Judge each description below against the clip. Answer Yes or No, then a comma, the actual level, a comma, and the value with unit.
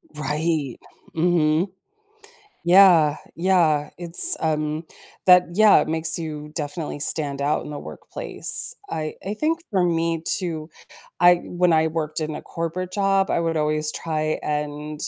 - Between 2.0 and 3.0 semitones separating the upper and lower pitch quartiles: Yes, narrow, 2.6 semitones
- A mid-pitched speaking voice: Yes, medium, 160 Hz